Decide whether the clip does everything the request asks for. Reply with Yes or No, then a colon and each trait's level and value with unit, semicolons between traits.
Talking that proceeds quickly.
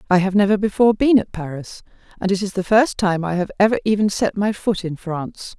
Yes: fast, 235 wpm